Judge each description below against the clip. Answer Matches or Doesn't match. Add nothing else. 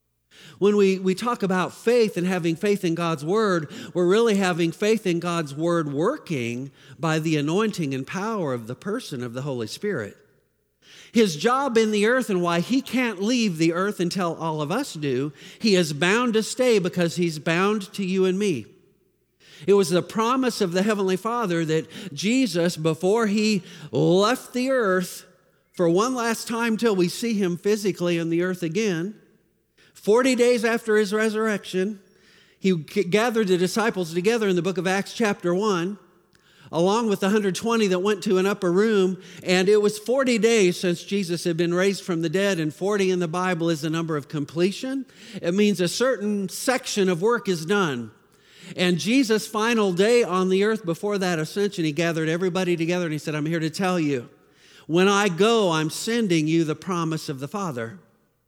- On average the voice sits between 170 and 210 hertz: Matches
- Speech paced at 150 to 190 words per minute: Matches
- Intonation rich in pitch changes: Doesn't match